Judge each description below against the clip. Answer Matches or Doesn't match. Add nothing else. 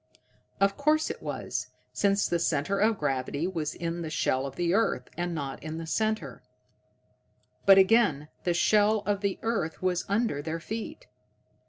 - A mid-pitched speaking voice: Matches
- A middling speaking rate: Matches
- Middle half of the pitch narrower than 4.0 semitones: Doesn't match